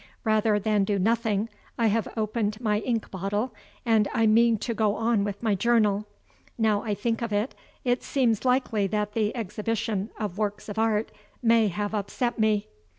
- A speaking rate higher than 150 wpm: Yes, average, 175 wpm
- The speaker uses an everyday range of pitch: No, narrow, 1.7 semitones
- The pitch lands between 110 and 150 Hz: No, high, 215 Hz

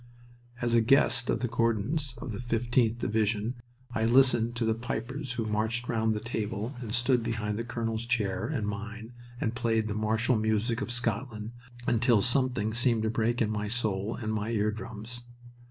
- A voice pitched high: No, low, 115 Hz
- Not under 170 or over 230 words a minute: Yes, average, 180 wpm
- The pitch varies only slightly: Yes, narrow, 1.8 semitones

